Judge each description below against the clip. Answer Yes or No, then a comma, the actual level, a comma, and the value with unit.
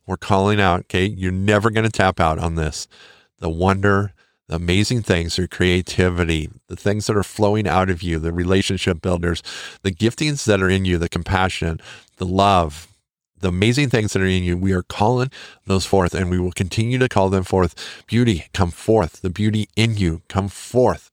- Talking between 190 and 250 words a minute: Yes, average, 195 wpm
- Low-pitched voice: Yes, very low, 95 Hz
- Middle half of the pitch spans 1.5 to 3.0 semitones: Yes, average, 2.7 semitones